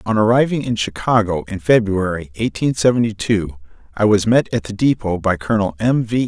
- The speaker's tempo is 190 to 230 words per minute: No, average, 180 wpm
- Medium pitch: No, low, 105 Hz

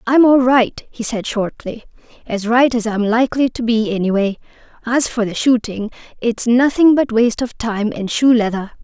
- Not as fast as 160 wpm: No, average, 175 wpm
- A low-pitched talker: No, high, 235 Hz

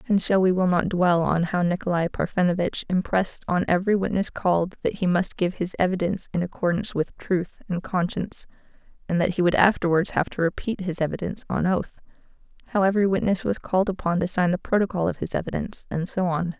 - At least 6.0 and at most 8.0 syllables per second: Yes, 6.1 syllables/s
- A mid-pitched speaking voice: Yes, medium, 180 Hz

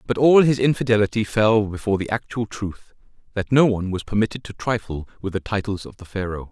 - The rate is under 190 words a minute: No, average, 195 wpm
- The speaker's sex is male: Yes, male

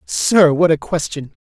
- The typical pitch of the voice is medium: Yes, medium, 160 Hz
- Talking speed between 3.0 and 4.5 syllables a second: Yes, 4.0 syllables/s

